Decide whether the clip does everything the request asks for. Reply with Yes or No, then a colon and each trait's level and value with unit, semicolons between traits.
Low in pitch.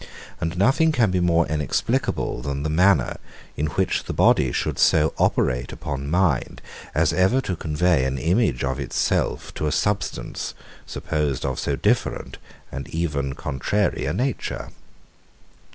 Yes: very low, 80 Hz